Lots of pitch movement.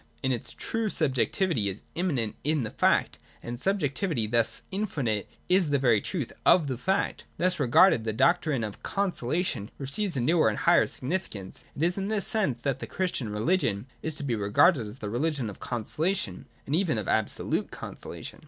Yes: wide, 7.9 semitones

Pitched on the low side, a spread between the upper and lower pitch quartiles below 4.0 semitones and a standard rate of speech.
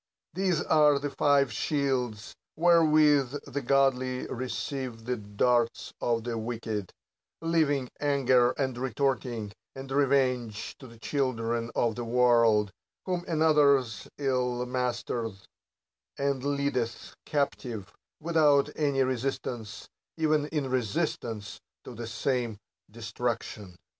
No: low, 130 Hz; average, 3.4 semitones; slow, 110 wpm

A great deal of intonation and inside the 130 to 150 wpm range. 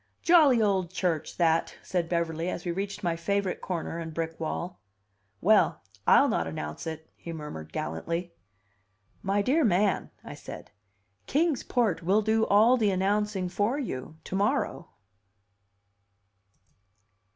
No: average, 4.0 semitones; slow, 135 wpm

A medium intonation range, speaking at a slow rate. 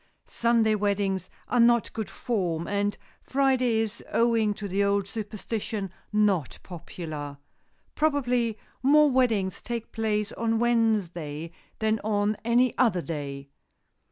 Yes: average, 3.5 semitones; slow, 120 wpm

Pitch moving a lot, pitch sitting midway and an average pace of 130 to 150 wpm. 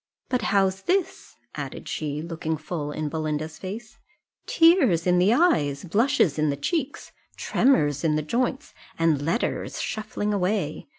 Yes: wide, 6.7 semitones; medium, 180 Hz; average, 140 wpm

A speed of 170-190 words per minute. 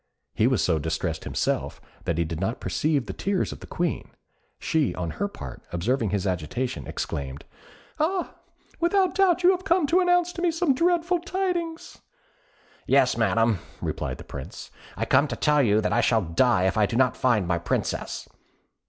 Yes: average, 180 wpm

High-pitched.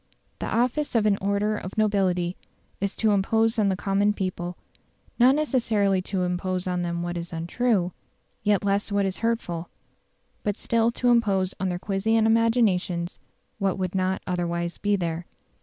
Yes: high, 195 Hz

